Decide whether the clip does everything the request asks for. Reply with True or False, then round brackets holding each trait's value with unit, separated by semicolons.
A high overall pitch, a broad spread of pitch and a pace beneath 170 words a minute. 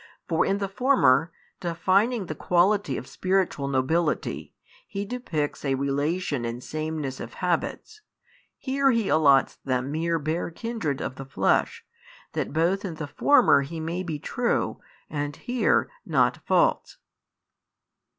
False (165 Hz; 5.7 semitones; 140 wpm)